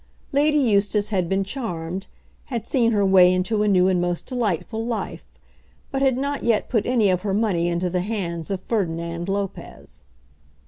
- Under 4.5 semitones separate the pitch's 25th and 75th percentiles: Yes, average, 4.1 semitones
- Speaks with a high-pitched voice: Yes, high, 200 Hz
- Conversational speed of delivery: Yes, average, 175 wpm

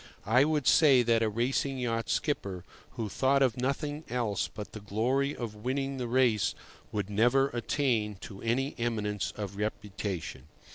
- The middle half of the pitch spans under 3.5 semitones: No, average, 4.1 semitones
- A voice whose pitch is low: Yes, low, 120 Hz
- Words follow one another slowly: No, average, 155 wpm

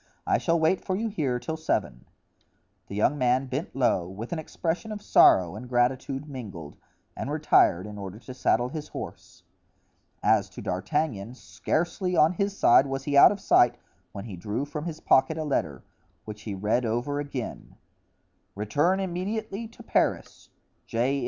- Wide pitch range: Yes, wide, 6.7 semitones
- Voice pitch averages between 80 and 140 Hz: Yes, low, 135 Hz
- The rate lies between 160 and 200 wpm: Yes, average, 165 wpm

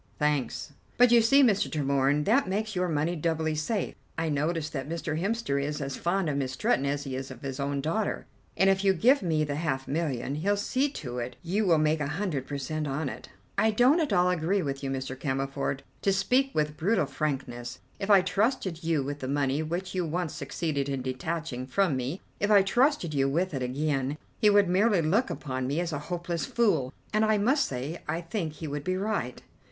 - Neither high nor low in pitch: Yes, medium, 160 Hz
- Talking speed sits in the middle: No, fast, 215 wpm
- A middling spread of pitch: No, wide, 5.7 semitones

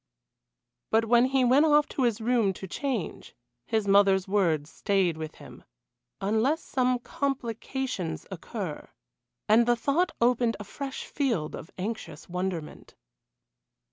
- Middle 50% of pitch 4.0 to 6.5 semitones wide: Yes, average, 5.0 semitones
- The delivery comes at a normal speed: No, slow, 130 wpm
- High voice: Yes, high, 225 Hz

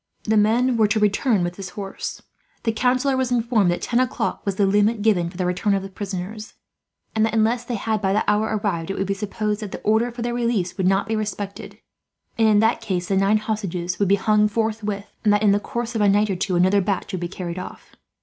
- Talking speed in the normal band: No, fast, 245 wpm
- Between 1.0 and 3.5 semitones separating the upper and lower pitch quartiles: Yes, narrow, 2.4 semitones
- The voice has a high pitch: Yes, high, 210 Hz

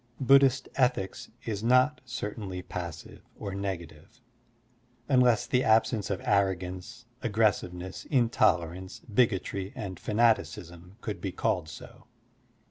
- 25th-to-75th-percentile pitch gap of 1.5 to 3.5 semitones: No, average, 4.5 semitones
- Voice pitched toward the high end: No, low, 100 Hz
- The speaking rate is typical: No, slow, 110 wpm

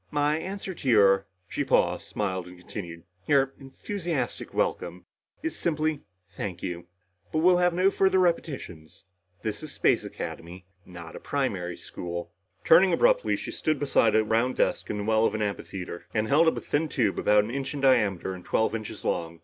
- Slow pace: No, average, 185 wpm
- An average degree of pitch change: No, wide, 8.9 semitones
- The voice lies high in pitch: No, low, 115 Hz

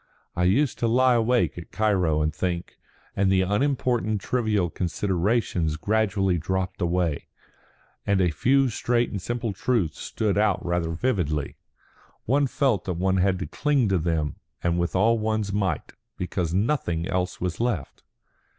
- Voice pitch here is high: No, very low, 95 Hz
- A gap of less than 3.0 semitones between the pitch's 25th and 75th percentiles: No, average, 4.7 semitones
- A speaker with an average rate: Yes, average, 150 wpm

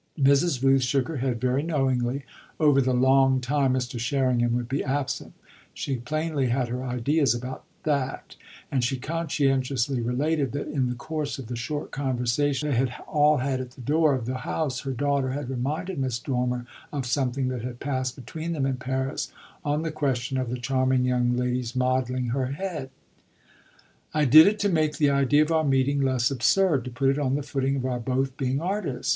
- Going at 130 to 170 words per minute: No, average, 195 wpm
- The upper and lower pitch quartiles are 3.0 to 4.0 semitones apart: No, narrow, 2.4 semitones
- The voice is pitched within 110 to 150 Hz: Yes, low, 135 Hz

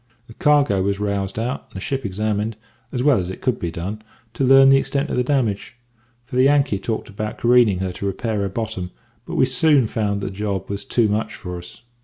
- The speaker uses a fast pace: Yes, fast, 230 wpm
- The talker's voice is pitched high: No, low, 110 Hz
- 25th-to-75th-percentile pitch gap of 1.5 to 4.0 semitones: No, average, 4.4 semitones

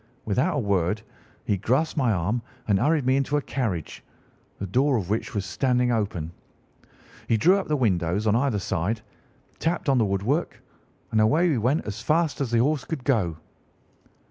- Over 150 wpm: Yes, average, 185 wpm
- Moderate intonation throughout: No, wide, 5.8 semitones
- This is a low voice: Yes, low, 120 Hz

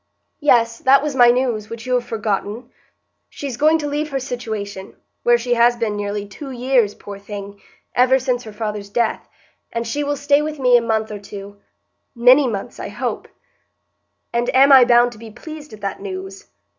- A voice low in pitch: No, high, 235 Hz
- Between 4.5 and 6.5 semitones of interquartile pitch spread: No, average, 4.1 semitones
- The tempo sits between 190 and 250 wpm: No, average, 180 wpm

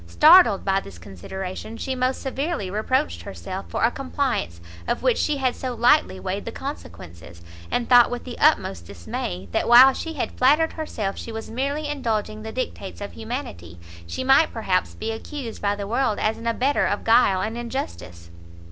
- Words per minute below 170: No, average, 180 wpm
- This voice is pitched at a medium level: No, high, 230 Hz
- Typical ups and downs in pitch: No, wide, 5.8 semitones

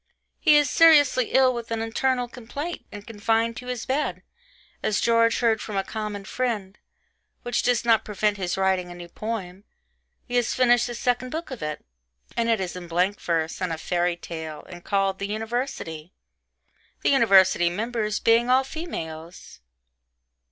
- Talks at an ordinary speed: Yes, average, 165 wpm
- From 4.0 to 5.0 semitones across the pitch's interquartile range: Yes, average, 4.7 semitones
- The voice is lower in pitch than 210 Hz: No, high, 220 Hz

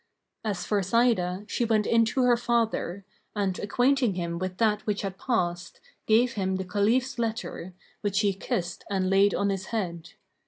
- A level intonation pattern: No, average, 3.5 semitones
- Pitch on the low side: No, high, 200 Hz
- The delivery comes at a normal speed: Yes, average, 170 wpm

